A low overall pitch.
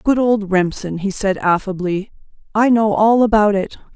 No: high, 205 Hz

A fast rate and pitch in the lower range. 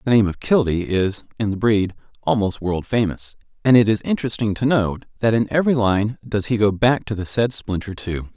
Yes: fast, 215 wpm; low, 110 Hz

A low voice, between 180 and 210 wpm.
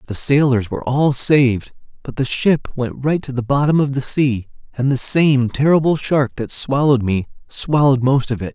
Yes: low, 130 Hz; average, 195 wpm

